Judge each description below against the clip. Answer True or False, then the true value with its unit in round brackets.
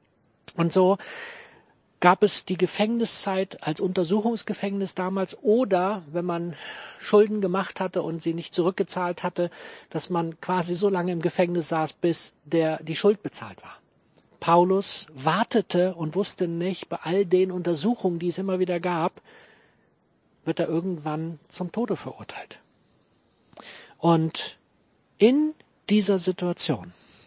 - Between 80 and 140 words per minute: True (130 wpm)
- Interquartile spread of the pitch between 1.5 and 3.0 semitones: True (2.6 semitones)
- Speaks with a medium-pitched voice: True (180 Hz)